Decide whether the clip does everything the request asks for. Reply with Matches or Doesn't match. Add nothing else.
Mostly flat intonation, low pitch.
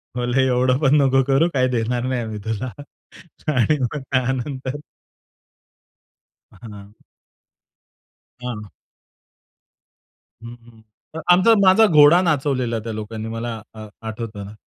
Doesn't match